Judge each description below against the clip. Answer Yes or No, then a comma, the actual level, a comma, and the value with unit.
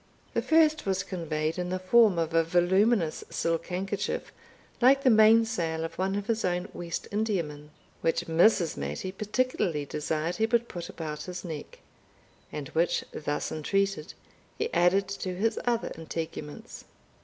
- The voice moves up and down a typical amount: Yes, average, 4.6 semitones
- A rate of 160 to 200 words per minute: No, average, 150 wpm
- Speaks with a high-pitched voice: No, medium, 180 Hz